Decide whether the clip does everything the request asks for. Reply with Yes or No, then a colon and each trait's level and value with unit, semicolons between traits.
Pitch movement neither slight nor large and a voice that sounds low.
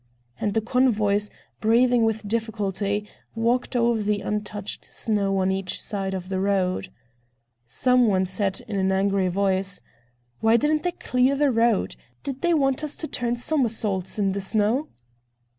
No: average, 3.8 semitones; high, 210 Hz